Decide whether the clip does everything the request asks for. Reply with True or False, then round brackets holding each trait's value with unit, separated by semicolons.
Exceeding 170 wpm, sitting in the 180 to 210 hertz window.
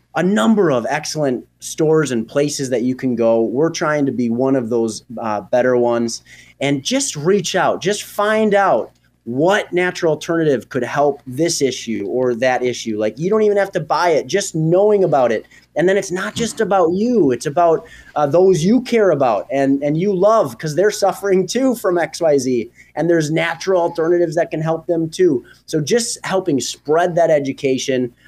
False (190 wpm; 160 Hz)